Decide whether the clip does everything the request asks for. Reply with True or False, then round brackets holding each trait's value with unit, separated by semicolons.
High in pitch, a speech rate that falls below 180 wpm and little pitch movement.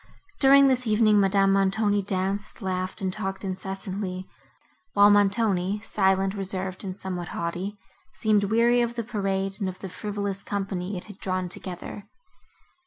True (195 Hz; 145 wpm; 1.7 semitones)